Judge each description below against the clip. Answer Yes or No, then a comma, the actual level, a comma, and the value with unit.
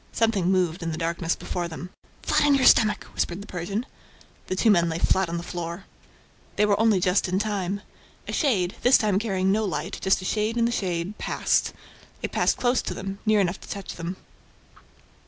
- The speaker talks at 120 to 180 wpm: No, fast, 205 wpm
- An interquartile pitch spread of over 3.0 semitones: Yes, average, 3.4 semitones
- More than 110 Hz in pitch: Yes, high, 190 Hz